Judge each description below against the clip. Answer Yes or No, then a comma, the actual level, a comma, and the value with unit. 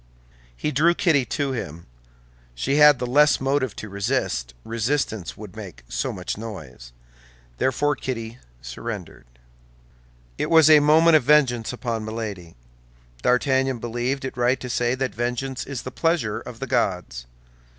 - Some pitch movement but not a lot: Yes, average, 4.1 semitones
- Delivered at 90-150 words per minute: Yes, average, 145 wpm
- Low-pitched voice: Yes, low, 125 Hz